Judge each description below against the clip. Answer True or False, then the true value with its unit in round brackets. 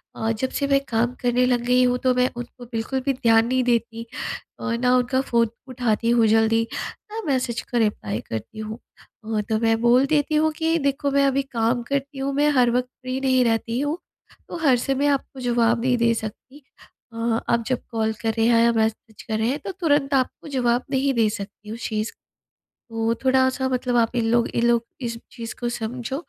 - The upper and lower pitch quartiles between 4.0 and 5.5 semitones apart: False (2.5 semitones)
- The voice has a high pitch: True (245 Hz)